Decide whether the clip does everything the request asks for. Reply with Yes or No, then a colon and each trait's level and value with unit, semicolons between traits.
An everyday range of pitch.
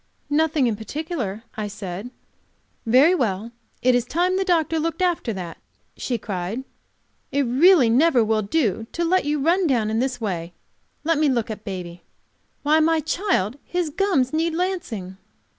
No: wide, 7.2 semitones